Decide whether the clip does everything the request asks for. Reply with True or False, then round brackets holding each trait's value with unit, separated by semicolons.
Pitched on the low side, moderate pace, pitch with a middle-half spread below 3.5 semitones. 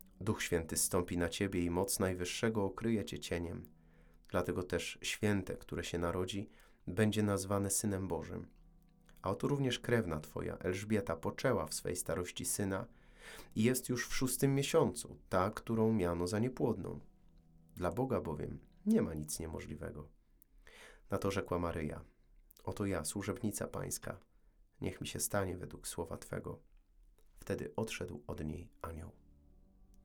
False (95 Hz; 140 wpm; 4.6 semitones)